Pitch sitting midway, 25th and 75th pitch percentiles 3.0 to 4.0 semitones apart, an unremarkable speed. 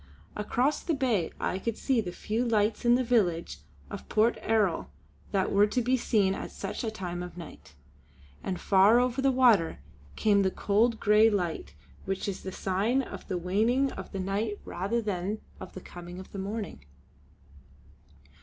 No: high, 205 Hz; average, 3.7 semitones; average, 175 wpm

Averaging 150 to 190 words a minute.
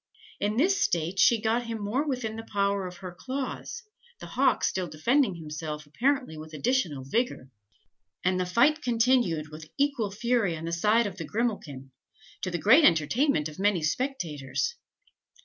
Yes: average, 160 wpm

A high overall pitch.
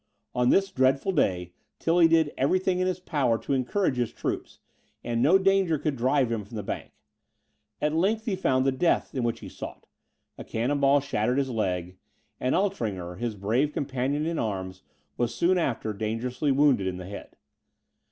No: low, 130 Hz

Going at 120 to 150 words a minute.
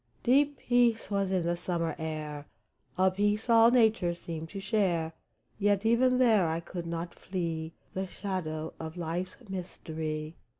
Yes: average, 145 wpm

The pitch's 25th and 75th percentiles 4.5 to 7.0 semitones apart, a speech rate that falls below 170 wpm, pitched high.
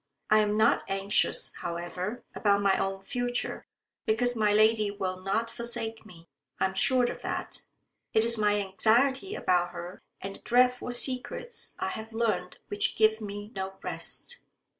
No: average, 3.4 semitones; average, 160 wpm; high, 215 Hz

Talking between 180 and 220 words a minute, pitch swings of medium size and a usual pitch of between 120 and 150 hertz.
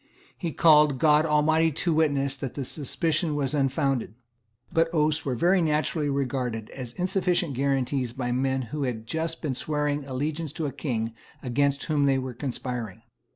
No: average, 160 wpm; average, 3.0 semitones; medium, 140 Hz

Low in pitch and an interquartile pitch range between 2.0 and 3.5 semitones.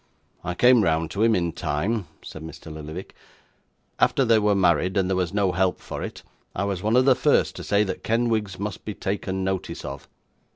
Yes: very low, 95 Hz; average, 3.2 semitones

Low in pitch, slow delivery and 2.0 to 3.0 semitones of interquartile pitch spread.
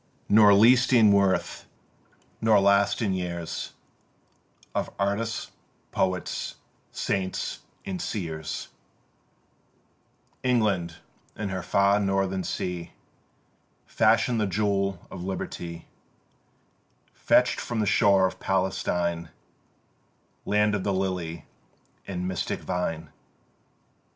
Yes: very low, 95 Hz; slow, 95 wpm; narrow, 2.6 semitones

